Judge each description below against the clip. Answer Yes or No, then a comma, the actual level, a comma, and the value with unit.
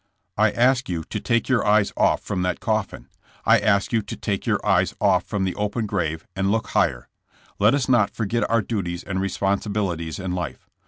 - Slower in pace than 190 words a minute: No, average, 200 wpm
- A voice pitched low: Yes, low, 100 Hz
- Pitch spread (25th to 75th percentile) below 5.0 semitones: Yes, average, 3.1 semitones